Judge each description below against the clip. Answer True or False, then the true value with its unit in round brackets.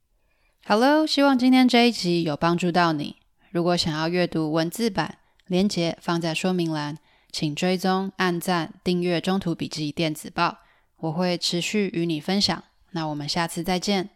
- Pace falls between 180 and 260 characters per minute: True (250 characters per minute)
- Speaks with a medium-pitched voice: True (175 Hz)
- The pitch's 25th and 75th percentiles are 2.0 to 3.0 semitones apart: True (2.6 semitones)